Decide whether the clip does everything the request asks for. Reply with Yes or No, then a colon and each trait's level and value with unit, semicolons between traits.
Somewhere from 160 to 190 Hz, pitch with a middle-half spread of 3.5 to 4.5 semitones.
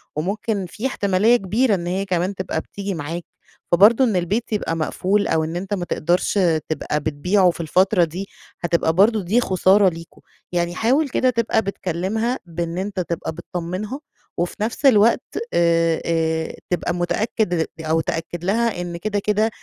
Yes: medium, 185 Hz; average, 3.8 semitones